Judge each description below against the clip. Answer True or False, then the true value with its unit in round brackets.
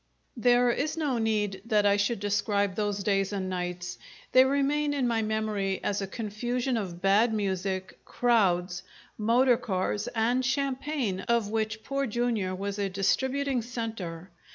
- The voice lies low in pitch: False (215 Hz)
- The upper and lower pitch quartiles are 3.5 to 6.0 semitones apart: True (3.8 semitones)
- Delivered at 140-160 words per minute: True (150 wpm)